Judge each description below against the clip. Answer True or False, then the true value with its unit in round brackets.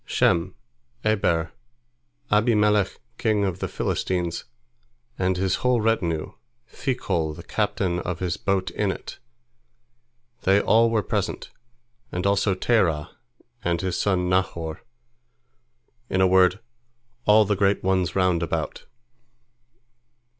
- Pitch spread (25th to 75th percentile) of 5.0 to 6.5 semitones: False (3.5 semitones)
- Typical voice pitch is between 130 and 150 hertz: False (95 Hz)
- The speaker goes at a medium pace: False (110 wpm)